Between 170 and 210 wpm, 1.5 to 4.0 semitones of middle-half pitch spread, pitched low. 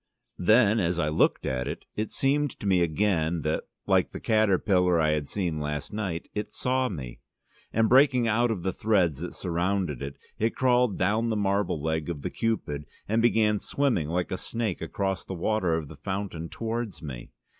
No: average, 190 wpm; wide, 5.4 semitones; very low, 95 Hz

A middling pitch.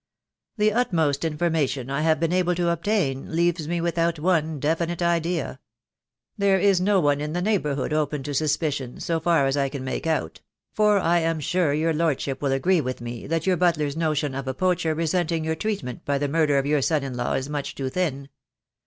Yes: medium, 160 Hz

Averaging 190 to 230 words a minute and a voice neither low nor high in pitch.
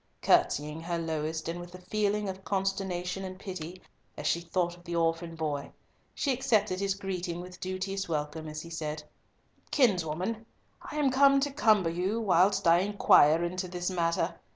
No: average, 170 wpm; medium, 180 Hz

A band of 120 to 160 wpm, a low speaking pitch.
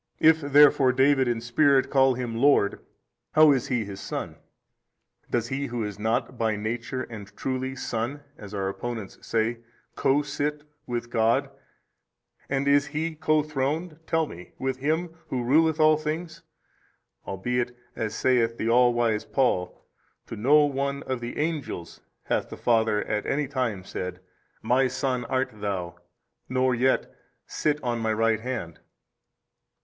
Yes: average, 155 wpm; low, 125 Hz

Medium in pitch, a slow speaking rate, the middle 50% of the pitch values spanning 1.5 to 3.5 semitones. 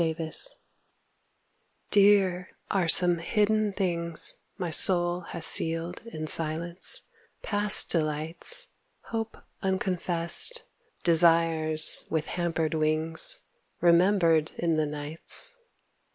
Yes: medium, 170 Hz; slow, 95 wpm; average, 2.8 semitones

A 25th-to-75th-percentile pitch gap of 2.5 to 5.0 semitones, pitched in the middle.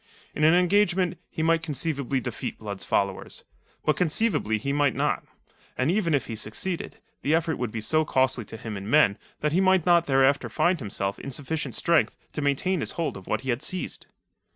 No: wide, 5.4 semitones; medium, 150 Hz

